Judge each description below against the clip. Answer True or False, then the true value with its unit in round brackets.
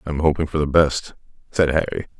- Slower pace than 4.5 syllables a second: False (5.6 syllables/s)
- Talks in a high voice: False (75 Hz)